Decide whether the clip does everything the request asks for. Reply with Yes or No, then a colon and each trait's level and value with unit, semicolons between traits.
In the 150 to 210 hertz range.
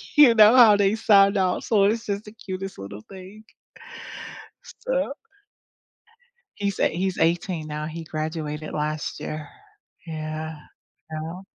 Yes: medium, 185 Hz